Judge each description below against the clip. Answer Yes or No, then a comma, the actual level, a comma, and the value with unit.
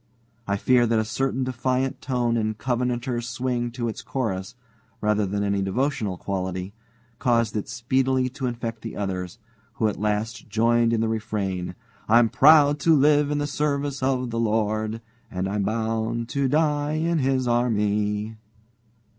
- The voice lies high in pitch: No, low, 115 Hz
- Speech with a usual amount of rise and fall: Yes, average, 3.6 semitones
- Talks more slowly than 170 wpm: Yes, average, 155 wpm